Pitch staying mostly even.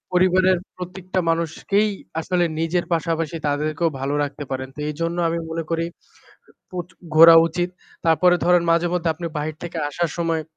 Yes: narrow, 1.9 semitones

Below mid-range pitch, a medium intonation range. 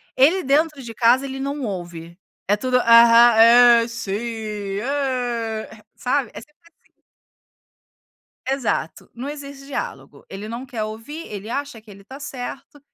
No: high, 245 Hz; average, 3.8 semitones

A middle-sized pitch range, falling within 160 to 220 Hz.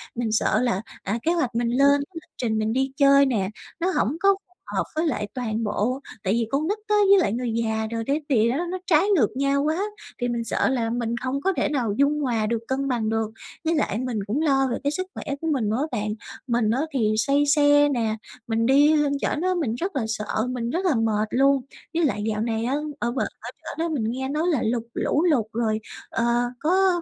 No: average, 4.6 semitones; very high, 255 Hz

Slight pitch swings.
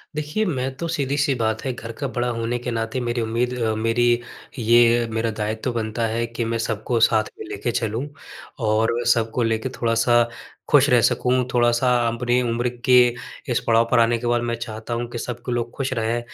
Yes: narrow, 1.5 semitones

